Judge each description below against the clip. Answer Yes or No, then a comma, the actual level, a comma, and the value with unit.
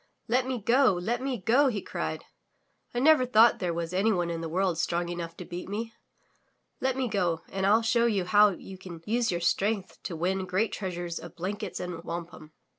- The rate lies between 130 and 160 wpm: No, average, 200 wpm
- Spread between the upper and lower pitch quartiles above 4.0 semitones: Yes, average, 4.7 semitones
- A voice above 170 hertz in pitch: Yes, high, 190 Hz